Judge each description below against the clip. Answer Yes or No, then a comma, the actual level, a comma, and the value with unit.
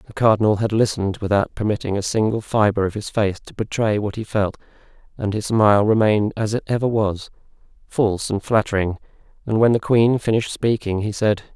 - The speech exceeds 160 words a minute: Yes, average, 180 wpm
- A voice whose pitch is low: Yes, low, 105 Hz